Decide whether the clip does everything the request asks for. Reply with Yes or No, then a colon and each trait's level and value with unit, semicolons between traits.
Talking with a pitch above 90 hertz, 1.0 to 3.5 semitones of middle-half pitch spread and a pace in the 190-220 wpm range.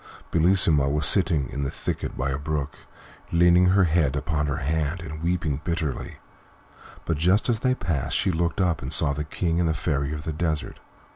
No: very low, 80 Hz; average, 3.0 semitones; average, 200 wpm